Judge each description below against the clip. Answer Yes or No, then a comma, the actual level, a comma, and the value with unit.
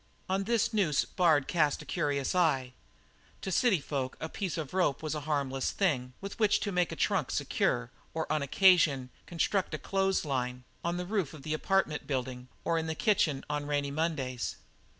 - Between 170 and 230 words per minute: Yes, average, 190 wpm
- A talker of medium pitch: Yes, medium, 155 Hz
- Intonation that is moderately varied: Yes, average, 4.9 semitones